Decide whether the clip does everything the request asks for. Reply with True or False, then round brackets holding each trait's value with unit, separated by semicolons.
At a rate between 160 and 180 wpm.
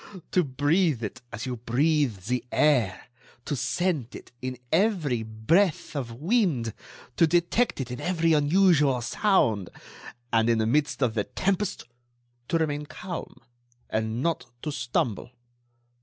False (140 wpm)